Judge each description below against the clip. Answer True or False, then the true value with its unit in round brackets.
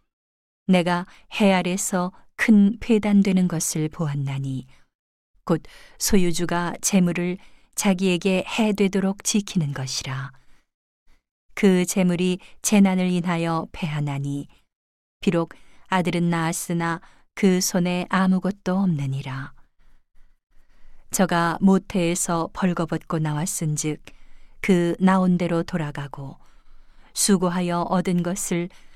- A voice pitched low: False (180 Hz)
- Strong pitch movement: False (2.5 semitones)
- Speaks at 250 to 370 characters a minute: False (215 characters per minute)